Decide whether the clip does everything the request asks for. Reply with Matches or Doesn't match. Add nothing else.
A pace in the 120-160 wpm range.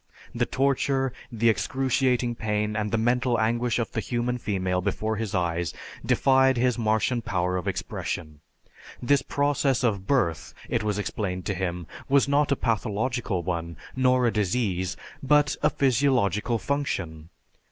Matches